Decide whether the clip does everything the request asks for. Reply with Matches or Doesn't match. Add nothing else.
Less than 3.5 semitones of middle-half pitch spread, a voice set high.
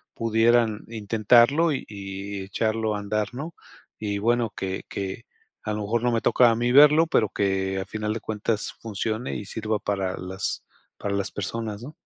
Doesn't match